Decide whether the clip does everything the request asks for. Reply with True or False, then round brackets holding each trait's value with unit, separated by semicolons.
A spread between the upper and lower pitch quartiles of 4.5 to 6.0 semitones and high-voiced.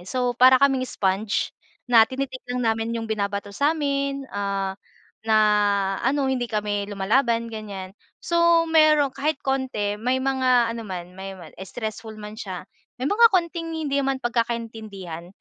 True (4.8 semitones; 235 Hz)